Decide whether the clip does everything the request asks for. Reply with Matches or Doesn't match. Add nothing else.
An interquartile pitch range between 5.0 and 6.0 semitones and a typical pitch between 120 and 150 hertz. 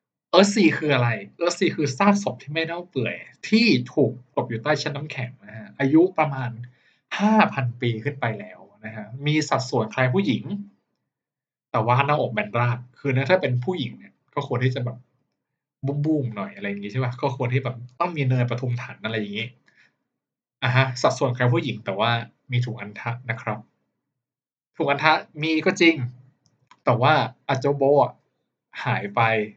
Doesn't match